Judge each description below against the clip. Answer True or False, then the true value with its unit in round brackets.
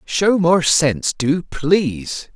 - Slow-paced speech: True (125 wpm)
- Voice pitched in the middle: True (160 Hz)